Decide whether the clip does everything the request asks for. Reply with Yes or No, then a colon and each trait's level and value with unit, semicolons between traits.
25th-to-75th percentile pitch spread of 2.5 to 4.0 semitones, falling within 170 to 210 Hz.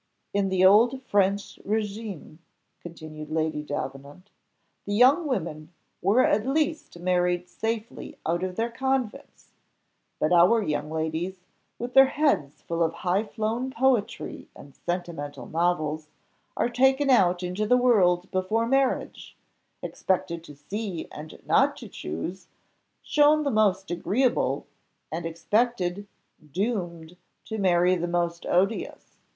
No: average, 5.2 semitones; medium, 185 Hz